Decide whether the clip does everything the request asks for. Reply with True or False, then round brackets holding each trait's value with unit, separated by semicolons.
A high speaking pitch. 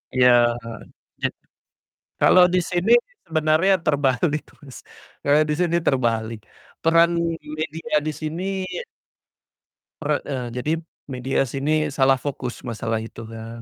False (145 Hz)